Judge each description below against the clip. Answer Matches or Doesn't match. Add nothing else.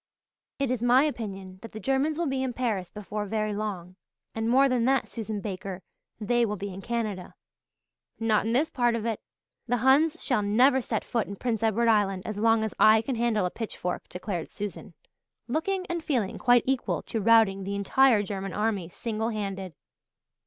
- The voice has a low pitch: Doesn't match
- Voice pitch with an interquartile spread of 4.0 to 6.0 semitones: Doesn't match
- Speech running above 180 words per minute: Matches